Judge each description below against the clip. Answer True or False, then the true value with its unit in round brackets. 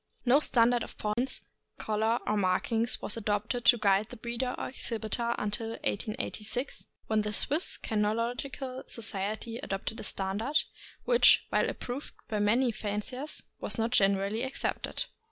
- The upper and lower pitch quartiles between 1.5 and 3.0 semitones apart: True (2.7 semitones)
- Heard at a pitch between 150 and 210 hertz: False (225 Hz)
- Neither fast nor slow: True (155 wpm)